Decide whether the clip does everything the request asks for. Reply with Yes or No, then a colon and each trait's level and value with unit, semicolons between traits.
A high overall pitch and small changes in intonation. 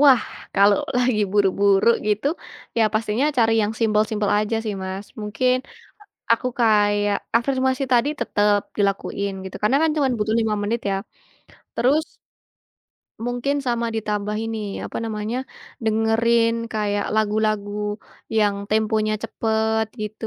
Yes: high, 220 Hz; narrow, 2.0 semitones